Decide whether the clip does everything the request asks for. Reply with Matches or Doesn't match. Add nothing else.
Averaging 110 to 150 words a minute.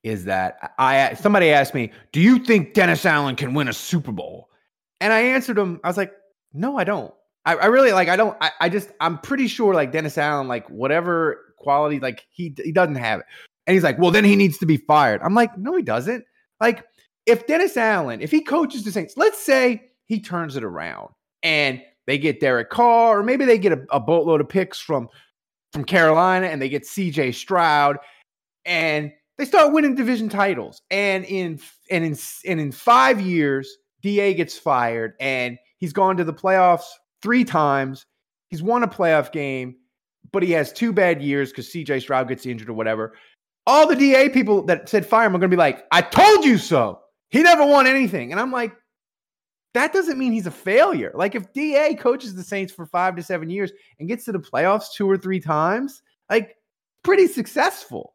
Doesn't match